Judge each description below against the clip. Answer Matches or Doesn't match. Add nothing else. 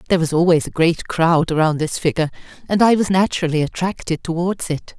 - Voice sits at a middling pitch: Matches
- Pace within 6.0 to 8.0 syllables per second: Matches